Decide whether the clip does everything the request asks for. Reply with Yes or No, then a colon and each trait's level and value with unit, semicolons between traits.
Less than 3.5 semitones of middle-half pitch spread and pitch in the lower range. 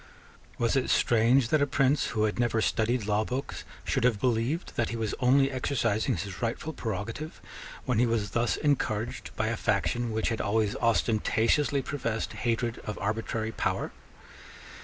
Yes: average, 2.8 semitones; low, 115 Hz